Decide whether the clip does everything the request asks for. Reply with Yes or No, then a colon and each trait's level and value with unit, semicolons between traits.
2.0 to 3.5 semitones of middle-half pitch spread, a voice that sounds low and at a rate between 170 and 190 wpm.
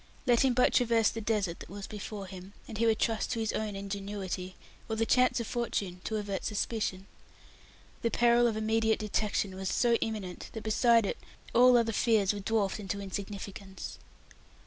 No: narrow, 2.5 semitones; high, 215 Hz; average, 180 wpm